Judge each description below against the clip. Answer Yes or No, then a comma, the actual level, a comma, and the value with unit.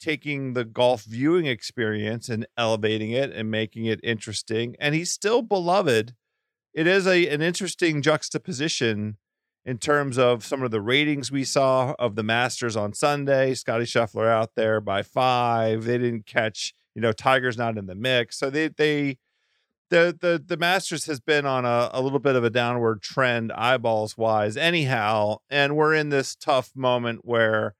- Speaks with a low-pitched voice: Yes, low, 125 Hz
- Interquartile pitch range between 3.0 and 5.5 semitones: Yes, average, 4.6 semitones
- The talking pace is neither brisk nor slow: Yes, average, 175 wpm